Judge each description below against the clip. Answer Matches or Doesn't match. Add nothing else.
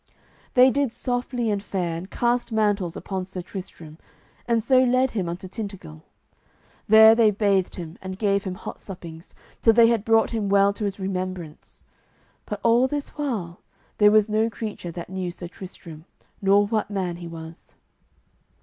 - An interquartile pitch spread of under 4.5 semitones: Matches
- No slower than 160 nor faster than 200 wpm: Matches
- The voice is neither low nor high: Doesn't match